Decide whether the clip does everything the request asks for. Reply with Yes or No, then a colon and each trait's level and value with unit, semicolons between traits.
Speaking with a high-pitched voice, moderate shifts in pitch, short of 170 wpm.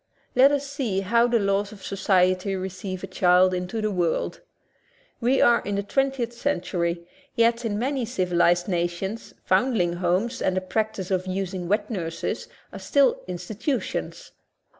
Yes: high, 195 Hz; average, 4.4 semitones; average, 155 wpm